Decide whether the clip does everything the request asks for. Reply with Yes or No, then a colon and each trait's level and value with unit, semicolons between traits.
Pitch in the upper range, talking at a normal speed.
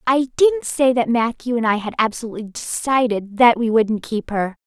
Yes: high, 235 Hz; average, 195 wpm